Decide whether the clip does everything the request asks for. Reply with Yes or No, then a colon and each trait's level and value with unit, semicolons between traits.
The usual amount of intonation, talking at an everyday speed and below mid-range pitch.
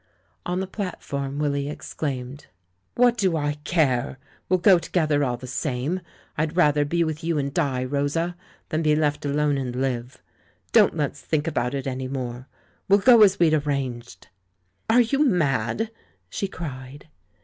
No: average, 4.4 semitones; average, 160 wpm; medium, 145 Hz